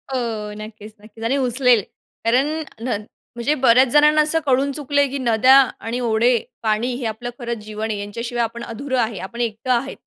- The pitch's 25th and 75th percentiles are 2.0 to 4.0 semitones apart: Yes, average, 2.9 semitones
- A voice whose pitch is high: Yes, high, 235 Hz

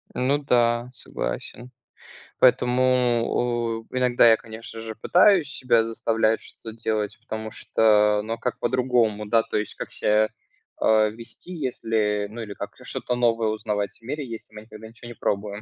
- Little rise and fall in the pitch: Yes, narrow, 2.2 semitones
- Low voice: Yes, low, 115 Hz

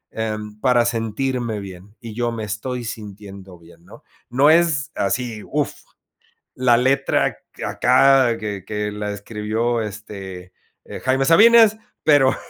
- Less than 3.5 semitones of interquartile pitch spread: No, average, 4.0 semitones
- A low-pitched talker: Yes, low, 115 Hz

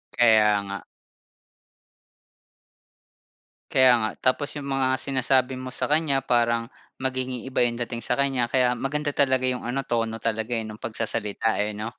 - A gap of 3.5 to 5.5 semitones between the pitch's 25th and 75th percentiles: No, average, 2.7 semitones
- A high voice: No, low, 125 Hz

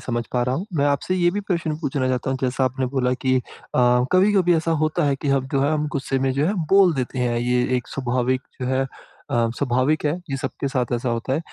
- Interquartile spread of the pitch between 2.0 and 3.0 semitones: No, average, 3.4 semitones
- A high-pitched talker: No, low, 135 Hz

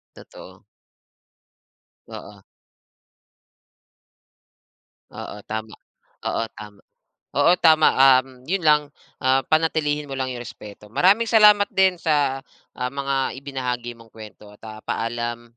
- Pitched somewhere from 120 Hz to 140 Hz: Yes, low, 135 Hz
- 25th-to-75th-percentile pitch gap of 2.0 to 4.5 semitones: No, average, 5.0 semitones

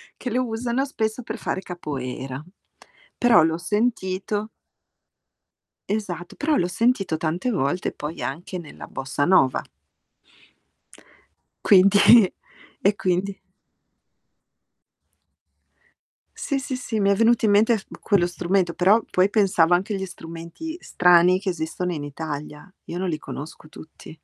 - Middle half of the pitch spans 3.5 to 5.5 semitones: Yes, average, 4.7 semitones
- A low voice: No, medium, 185 Hz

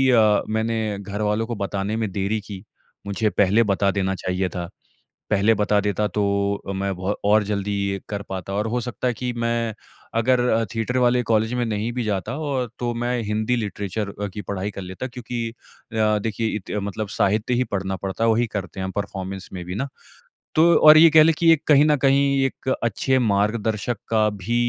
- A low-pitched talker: Yes, low, 105 Hz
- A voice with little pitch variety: No, average, 3.2 semitones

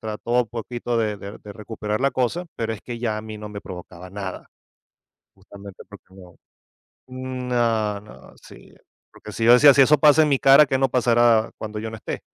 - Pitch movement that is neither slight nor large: Yes, average, 3.2 semitones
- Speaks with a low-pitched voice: Yes, low, 115 Hz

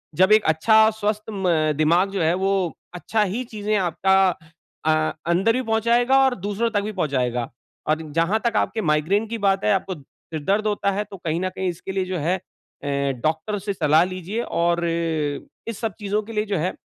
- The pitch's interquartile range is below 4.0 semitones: No, average, 4.5 semitones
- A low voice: No, high, 190 Hz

